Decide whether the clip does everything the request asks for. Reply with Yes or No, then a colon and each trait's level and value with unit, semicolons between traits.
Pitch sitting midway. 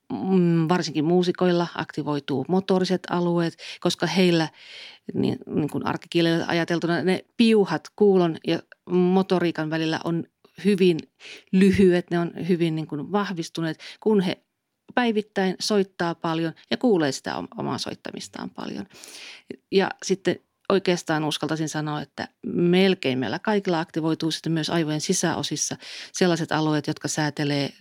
Yes: medium, 170 Hz